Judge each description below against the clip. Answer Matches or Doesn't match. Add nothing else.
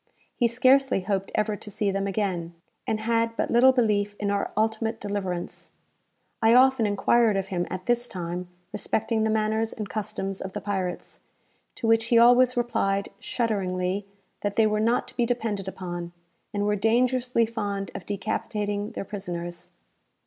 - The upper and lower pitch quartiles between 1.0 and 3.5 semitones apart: Matches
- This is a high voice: Matches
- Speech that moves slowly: Doesn't match